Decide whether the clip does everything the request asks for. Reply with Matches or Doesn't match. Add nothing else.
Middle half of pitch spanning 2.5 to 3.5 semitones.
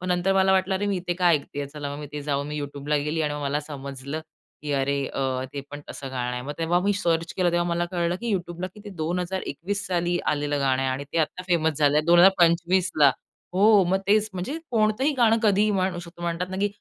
Doesn't match